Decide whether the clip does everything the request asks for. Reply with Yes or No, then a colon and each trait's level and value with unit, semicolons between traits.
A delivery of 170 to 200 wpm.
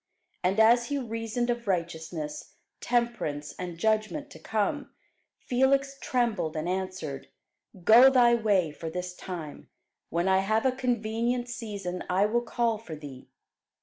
No: average, 140 wpm